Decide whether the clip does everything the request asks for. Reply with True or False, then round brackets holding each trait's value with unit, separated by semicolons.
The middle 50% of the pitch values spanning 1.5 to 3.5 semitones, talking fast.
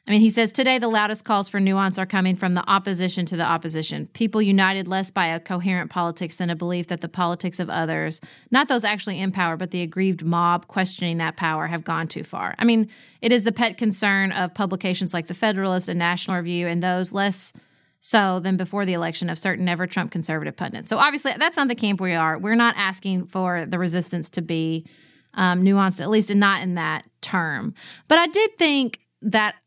True (3.2 semitones; 215 wpm)